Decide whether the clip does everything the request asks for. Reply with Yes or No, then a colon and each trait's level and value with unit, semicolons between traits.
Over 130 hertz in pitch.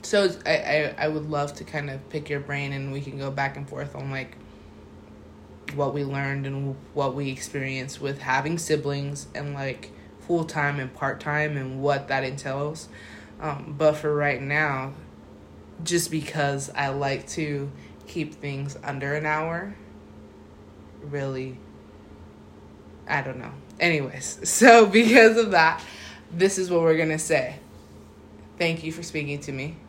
Yes: medium, 140 Hz